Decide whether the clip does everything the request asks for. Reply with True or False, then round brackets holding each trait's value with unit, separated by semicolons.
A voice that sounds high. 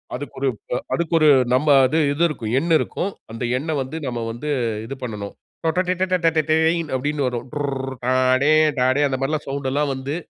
False (145 Hz)